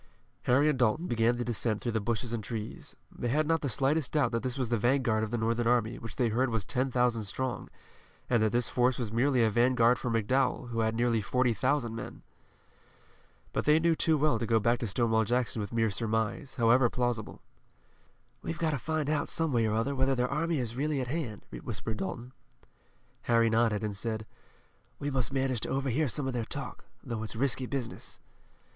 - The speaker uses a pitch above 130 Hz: No, low, 120 Hz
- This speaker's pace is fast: Yes, fast, 210 wpm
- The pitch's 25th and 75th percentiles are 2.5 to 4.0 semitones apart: Yes, average, 2.9 semitones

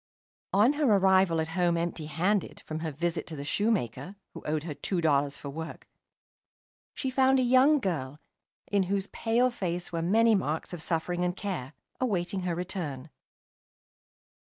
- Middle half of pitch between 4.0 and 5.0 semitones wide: Yes, average, 4.3 semitones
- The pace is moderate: Yes, average, 160 wpm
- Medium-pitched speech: Yes, medium, 175 Hz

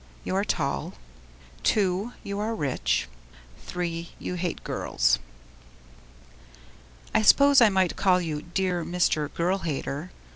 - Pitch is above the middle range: No, medium, 180 Hz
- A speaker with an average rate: No, slow, 120 wpm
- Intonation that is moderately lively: Yes, average, 4.1 semitones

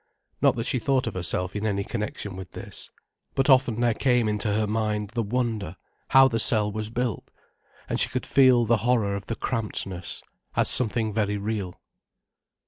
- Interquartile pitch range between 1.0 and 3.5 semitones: Yes, average, 2.8 semitones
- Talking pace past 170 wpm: Yes, average, 180 wpm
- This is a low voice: Yes, low, 110 Hz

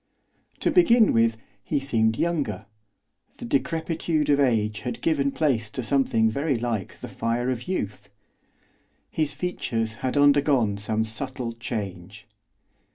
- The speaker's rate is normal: No, slow, 130 wpm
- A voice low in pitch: Yes, low, 125 Hz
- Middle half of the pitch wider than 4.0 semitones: Yes, average, 4.5 semitones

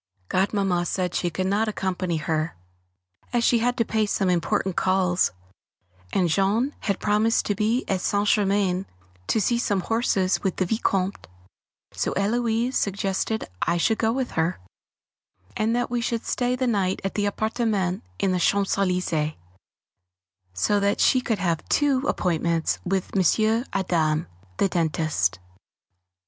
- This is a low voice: No, high, 195 Hz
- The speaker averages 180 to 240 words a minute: No, average, 150 wpm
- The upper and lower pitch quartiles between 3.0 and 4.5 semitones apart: Yes, average, 3.7 semitones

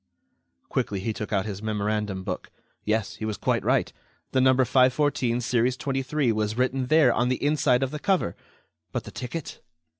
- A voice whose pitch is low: Yes, low, 125 Hz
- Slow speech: No, average, 175 wpm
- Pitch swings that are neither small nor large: Yes, average, 3.7 semitones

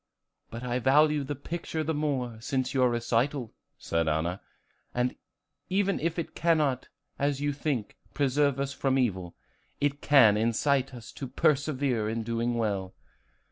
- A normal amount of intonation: Yes, average, 3.9 semitones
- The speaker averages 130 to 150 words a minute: Yes, average, 140 wpm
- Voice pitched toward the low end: Yes, low, 130 Hz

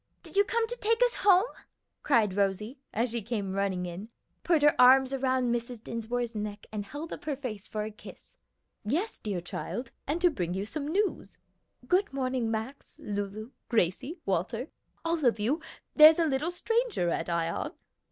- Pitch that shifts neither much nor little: No, wide, 6.8 semitones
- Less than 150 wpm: No, average, 175 wpm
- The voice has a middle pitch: No, high, 245 Hz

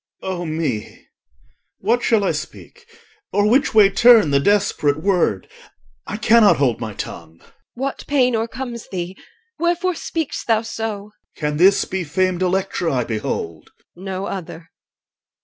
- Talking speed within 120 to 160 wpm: Yes, average, 150 wpm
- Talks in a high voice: Yes, high, 195 Hz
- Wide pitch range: Yes, wide, 6.0 semitones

